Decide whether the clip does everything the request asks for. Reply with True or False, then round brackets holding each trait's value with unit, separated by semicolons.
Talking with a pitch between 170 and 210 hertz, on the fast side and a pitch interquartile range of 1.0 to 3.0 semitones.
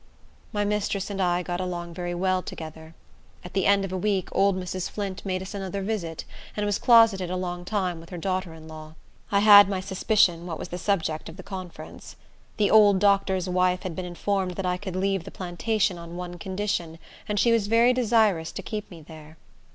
True (185 Hz; 210 wpm; 2.4 semitones)